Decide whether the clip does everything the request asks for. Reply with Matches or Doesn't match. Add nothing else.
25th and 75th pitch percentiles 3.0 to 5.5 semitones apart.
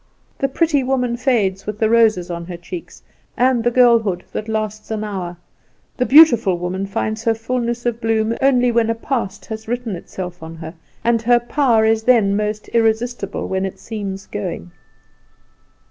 Matches